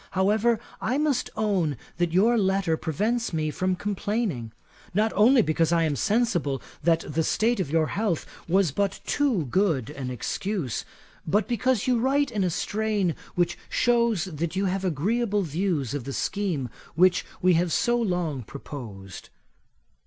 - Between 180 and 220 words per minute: No, average, 155 wpm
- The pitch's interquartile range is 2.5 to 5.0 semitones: No, wide, 5.5 semitones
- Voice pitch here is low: No, medium, 185 Hz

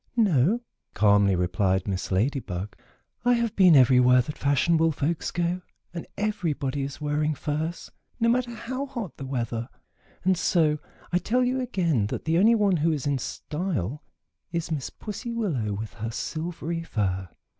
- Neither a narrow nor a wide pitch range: No, wide, 7.4 semitones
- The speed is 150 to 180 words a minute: Yes, average, 160 wpm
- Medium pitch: Yes, medium, 155 Hz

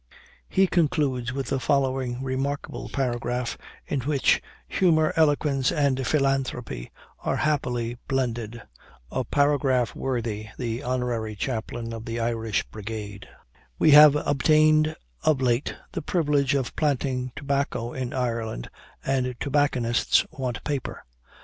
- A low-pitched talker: Yes, low, 130 Hz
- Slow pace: Yes, slow, 120 wpm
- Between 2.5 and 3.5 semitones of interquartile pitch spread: Yes, average, 3.2 semitones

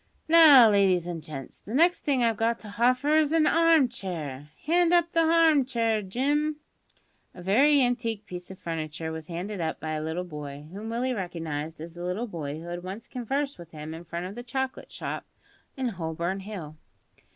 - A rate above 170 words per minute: Yes, average, 190 wpm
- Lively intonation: Yes, wide, 7.8 semitones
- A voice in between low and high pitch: No, high, 200 Hz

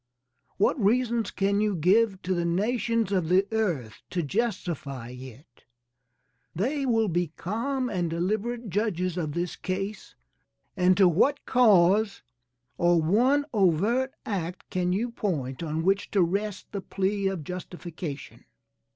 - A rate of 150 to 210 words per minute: No, slow, 135 wpm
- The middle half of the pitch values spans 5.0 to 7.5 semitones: No, average, 4.2 semitones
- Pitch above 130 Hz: Yes, high, 190 Hz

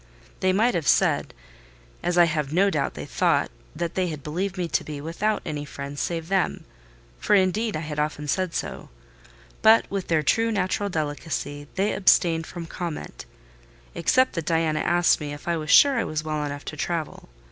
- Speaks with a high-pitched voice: No, medium, 165 Hz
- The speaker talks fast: No, average, 190 wpm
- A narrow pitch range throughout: No, average, 3.8 semitones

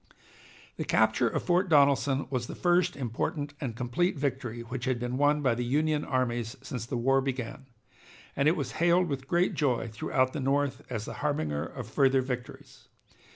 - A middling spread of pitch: Yes, average, 3.0 semitones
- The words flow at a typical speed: Yes, average, 180 wpm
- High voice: No, low, 135 Hz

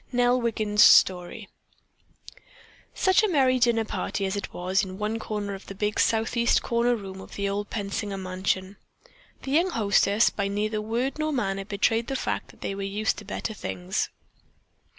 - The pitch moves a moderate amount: Yes, average, 3.1 semitones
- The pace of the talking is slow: No, average, 170 wpm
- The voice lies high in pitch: Yes, high, 210 Hz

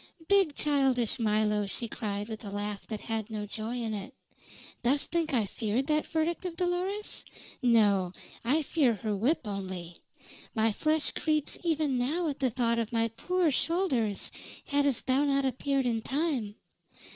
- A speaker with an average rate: Yes, average, 155 wpm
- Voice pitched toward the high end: Yes, high, 245 Hz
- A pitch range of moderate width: No, wide, 5.9 semitones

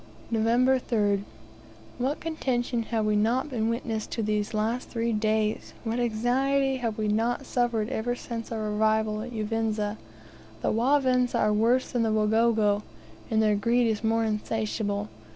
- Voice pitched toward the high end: Yes, high, 225 Hz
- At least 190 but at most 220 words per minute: No, average, 155 wpm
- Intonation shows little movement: Yes, narrow, 2.2 semitones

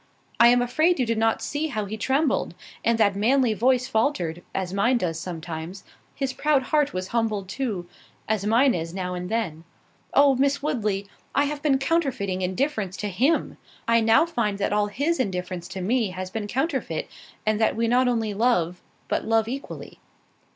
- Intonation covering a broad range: Yes, wide, 5.7 semitones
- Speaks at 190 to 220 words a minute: No, average, 175 wpm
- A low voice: No, high, 225 Hz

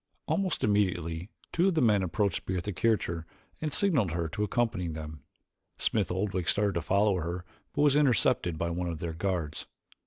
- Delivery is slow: No, average, 175 wpm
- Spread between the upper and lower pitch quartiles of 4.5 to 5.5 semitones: No, average, 4.1 semitones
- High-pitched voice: No, very low, 95 Hz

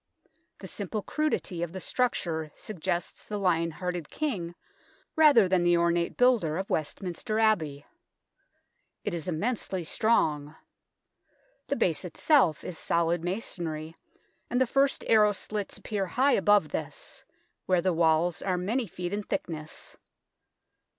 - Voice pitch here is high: No, medium, 180 Hz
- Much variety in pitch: No, average, 4.4 semitones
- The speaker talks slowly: Yes, slow, 130 wpm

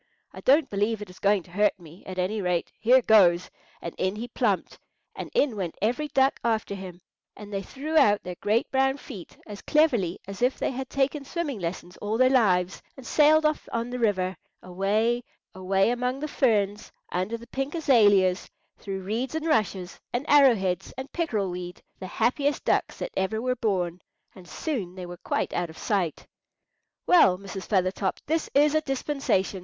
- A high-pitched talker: Yes, high, 210 Hz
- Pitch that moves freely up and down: Yes, wide, 6.0 semitones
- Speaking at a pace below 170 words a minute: No, average, 185 wpm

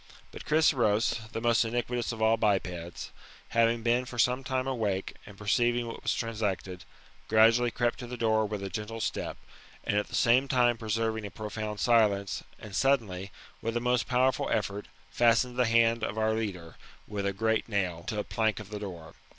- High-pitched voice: No, low, 110 Hz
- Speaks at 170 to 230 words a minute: Yes, average, 185 wpm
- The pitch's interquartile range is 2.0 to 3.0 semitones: Yes, narrow, 2.5 semitones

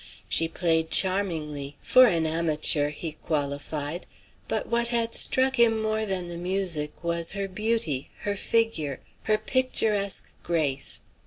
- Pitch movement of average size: No, wide, 5.9 semitones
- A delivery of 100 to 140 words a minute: Yes, slow, 135 wpm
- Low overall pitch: No, medium, 175 Hz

